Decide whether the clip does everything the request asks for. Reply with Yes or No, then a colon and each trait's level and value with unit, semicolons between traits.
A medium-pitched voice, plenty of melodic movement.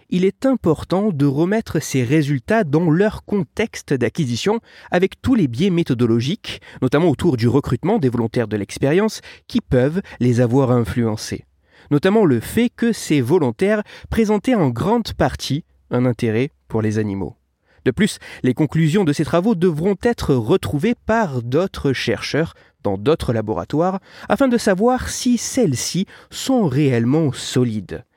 Yes: medium, 160 Hz; wide, 8.8 semitones